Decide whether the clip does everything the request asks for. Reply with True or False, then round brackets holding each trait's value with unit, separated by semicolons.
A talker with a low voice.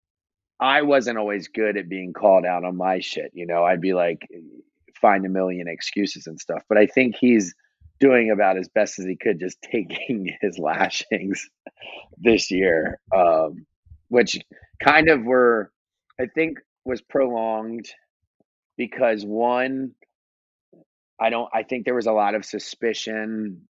True (105 Hz)